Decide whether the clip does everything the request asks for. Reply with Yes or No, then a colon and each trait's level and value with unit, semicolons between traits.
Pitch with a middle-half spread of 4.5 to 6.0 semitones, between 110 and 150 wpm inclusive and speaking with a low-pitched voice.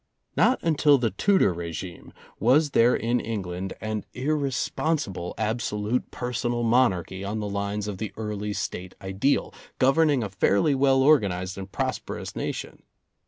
Yes: average, 5.2 semitones; average, 140 wpm; low, 110 Hz